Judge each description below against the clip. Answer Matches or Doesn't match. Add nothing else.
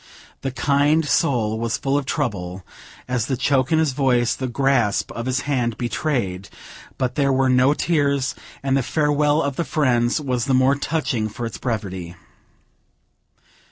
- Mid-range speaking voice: Doesn't match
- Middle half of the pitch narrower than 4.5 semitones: Matches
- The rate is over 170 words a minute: Doesn't match